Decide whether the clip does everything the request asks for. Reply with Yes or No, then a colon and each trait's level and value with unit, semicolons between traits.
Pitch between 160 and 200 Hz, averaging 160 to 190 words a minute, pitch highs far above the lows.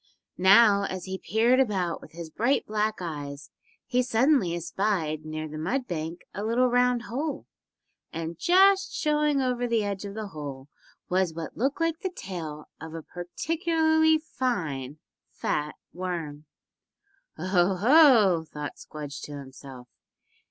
No: high, 190 Hz; average, 140 wpm; wide, 8.0 semitones